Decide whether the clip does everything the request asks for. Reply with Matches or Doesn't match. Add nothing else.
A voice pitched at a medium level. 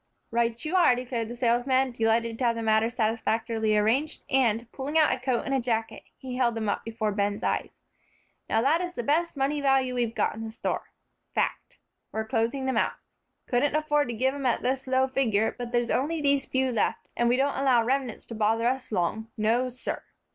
Doesn't match